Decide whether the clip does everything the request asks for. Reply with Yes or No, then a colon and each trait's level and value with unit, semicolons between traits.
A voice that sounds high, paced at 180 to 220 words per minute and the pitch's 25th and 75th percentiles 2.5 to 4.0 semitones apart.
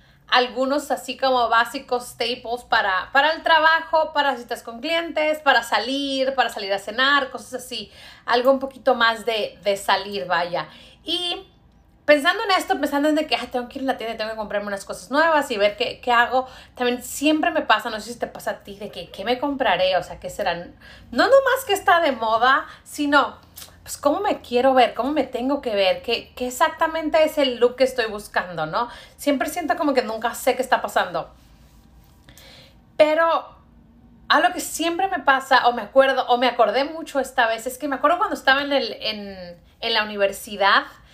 No: very high, 250 Hz; average, 200 wpm; average, 4.4 semitones